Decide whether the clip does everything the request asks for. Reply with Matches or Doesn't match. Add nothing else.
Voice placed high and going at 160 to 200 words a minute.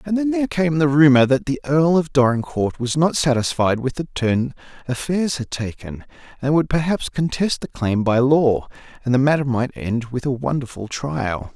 Doesn't match